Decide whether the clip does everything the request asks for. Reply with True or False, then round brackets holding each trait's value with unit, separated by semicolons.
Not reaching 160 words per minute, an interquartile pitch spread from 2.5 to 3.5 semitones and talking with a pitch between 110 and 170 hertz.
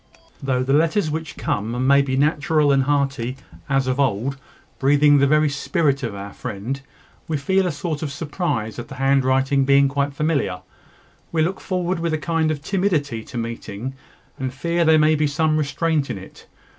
False (180 wpm; 2.9 semitones; 140 Hz)